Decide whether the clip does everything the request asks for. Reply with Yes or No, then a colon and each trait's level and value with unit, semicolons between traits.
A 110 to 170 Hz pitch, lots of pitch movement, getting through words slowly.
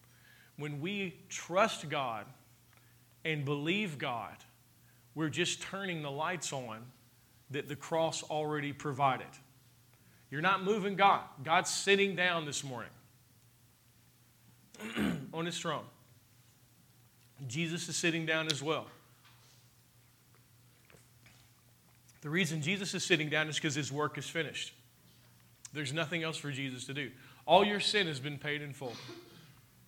No: medium, 140 Hz; average, 4.9 semitones; slow, 125 wpm